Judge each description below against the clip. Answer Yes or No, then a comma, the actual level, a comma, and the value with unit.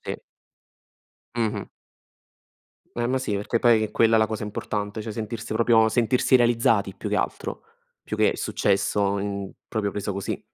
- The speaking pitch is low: Yes, low, 110 Hz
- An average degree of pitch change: No, narrow, 2.2 semitones